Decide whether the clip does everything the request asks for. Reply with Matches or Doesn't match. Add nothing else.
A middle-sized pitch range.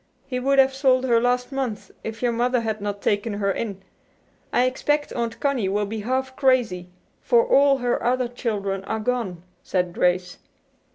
Matches